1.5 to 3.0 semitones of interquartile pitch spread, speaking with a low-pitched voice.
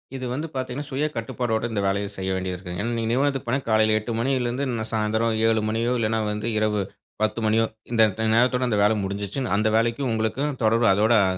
Yes: narrow, 2.6 semitones; low, 115 Hz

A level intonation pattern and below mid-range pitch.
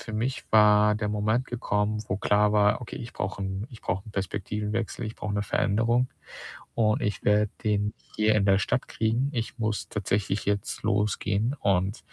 Yes: narrow, 1.4 semitones; low, 105 Hz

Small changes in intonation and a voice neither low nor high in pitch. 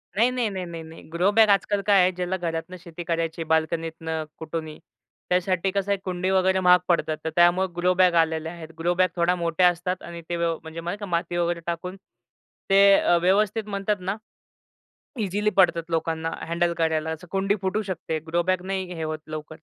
Yes: narrow, 2.3 semitones; medium, 175 Hz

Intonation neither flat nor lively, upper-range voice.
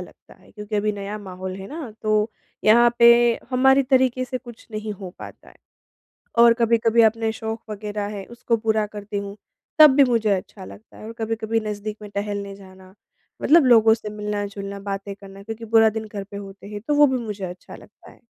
No: narrow, 2.3 semitones; high, 215 Hz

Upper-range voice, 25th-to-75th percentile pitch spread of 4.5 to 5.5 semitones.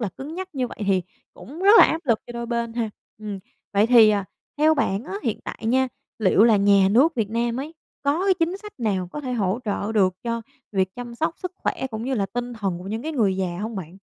Yes: high, 230 Hz; average, 5.0 semitones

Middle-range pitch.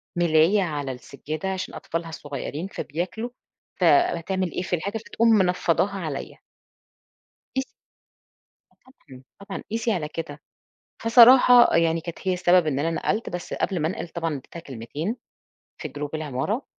Yes: medium, 170 Hz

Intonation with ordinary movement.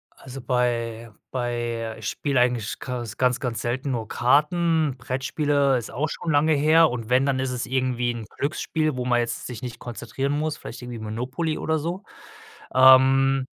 Yes: average, 3.0 semitones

